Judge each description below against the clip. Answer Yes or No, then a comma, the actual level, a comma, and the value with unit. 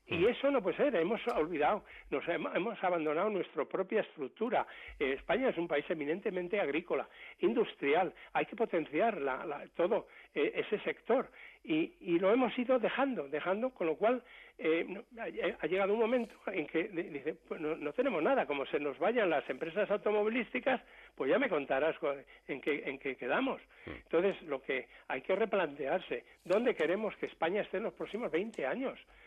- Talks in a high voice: Yes, high, 220 Hz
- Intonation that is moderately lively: No, wide, 7.7 semitones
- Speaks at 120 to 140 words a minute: No, average, 170 wpm